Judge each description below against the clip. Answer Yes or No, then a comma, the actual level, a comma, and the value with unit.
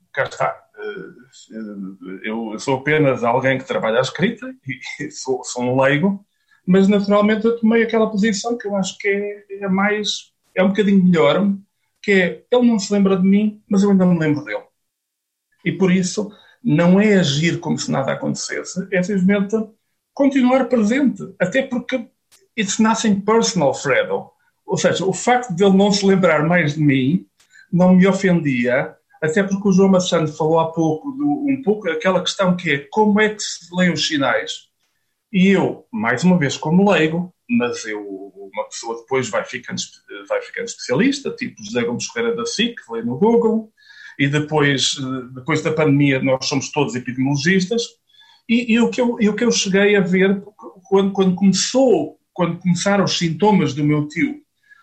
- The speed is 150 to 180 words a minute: Yes, average, 175 wpm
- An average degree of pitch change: No, wide, 6.2 semitones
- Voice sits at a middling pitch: No, high, 195 Hz